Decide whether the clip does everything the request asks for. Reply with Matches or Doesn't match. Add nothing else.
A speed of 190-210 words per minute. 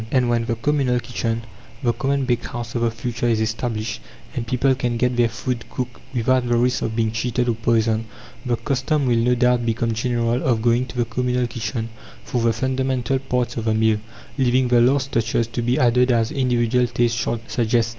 Matches